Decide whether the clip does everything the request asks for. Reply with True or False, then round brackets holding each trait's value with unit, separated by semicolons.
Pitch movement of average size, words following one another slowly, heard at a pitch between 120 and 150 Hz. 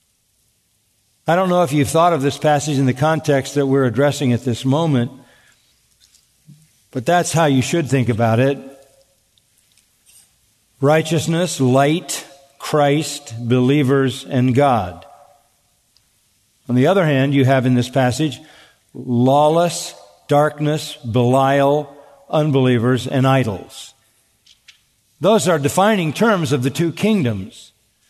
True (3.6 semitones; 115 wpm; 135 Hz)